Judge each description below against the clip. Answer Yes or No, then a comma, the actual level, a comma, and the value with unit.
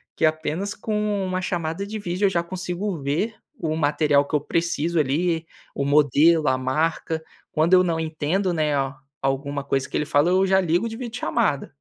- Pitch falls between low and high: Yes, medium, 165 Hz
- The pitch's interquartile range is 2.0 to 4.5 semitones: Yes, average, 4.1 semitones